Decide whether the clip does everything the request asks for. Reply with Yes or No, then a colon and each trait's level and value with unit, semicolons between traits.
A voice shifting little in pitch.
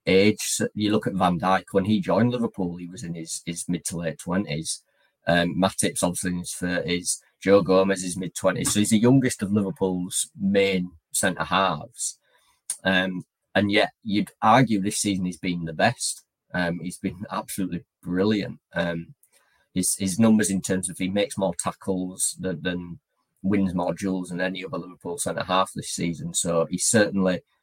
Yes: narrow, 2.0 semitones